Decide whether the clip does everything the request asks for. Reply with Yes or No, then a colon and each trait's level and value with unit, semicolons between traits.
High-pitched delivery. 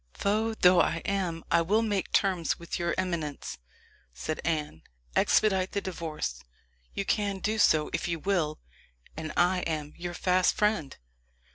No: medium, 175 Hz